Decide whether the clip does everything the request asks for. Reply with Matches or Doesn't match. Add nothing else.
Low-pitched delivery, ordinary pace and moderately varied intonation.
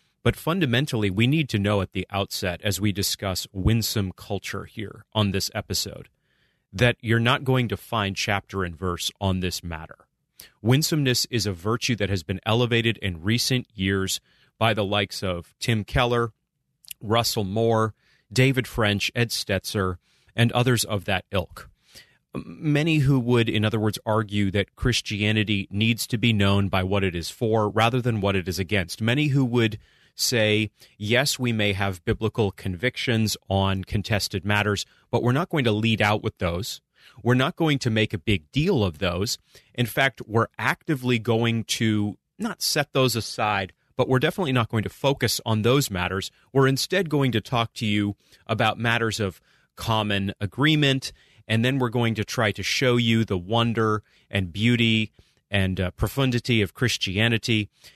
Matches